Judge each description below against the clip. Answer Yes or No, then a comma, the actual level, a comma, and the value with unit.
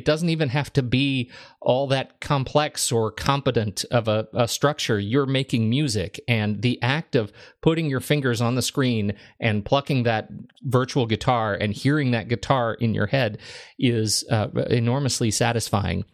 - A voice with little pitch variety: No, average, 3.9 semitones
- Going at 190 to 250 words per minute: No, average, 165 wpm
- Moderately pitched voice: No, low, 125 Hz